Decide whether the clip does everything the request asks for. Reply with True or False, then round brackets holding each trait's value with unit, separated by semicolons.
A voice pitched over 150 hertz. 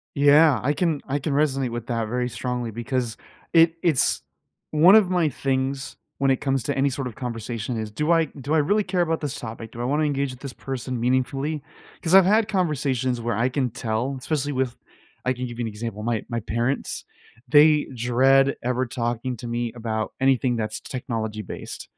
False (130 Hz)